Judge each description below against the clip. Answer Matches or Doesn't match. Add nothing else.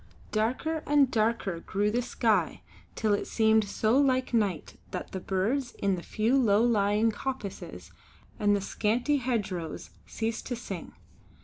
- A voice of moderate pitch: Doesn't match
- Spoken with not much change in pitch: Doesn't match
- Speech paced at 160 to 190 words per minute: Doesn't match